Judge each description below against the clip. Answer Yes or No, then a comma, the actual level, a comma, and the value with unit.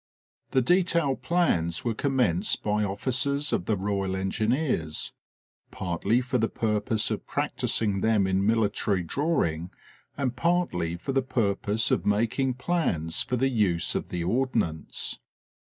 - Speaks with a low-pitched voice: Yes, low, 110 Hz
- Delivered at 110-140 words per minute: Yes, slow, 135 wpm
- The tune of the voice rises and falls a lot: Yes, wide, 5.7 semitones